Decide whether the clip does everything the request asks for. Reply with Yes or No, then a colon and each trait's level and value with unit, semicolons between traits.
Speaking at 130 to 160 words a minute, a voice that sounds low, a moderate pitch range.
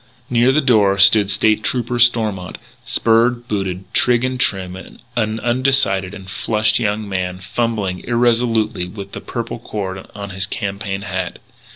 Yes: average, 145 wpm; low, 105 Hz; average, 3.5 semitones